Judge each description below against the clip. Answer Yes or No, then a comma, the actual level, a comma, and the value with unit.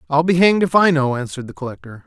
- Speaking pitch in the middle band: Yes, medium, 155 Hz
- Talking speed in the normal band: No, fast, 260 wpm